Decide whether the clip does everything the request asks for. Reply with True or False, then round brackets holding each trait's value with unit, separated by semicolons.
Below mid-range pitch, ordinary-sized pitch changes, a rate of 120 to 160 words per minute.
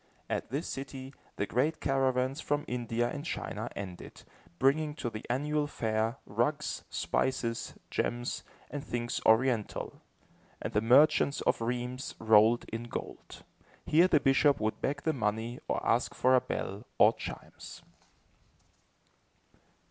True (125 Hz; 3.8 semitones; 135 wpm)